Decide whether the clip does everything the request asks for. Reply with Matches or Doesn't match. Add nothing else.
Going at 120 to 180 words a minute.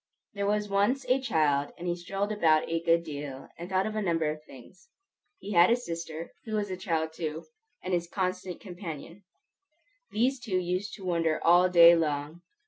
Doesn't match